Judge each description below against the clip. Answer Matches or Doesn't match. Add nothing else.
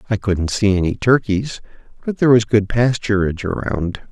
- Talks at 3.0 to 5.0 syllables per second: Doesn't match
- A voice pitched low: Matches